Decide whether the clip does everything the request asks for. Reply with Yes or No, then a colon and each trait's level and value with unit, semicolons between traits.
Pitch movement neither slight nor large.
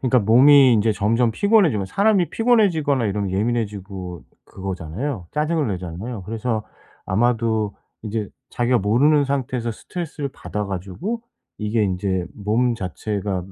No: wide, 5.7 semitones